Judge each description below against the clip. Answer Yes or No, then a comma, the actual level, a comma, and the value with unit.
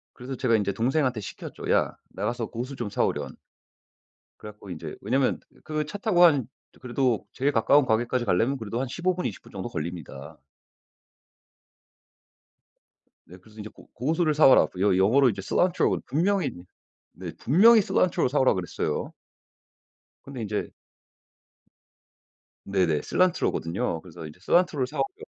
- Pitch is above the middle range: No, low, 120 Hz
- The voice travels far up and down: Yes, wide, 6.7 semitones